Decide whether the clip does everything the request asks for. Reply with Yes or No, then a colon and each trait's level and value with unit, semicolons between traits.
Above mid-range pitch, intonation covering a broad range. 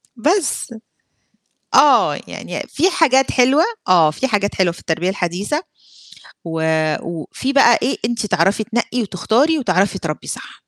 Yes: high, 215 Hz; wide, 7.3 semitones